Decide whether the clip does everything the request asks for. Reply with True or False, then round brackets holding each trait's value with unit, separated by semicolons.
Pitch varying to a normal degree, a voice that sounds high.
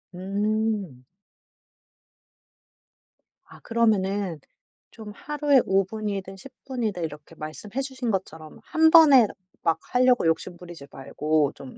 False (6.6 semitones; 200 Hz)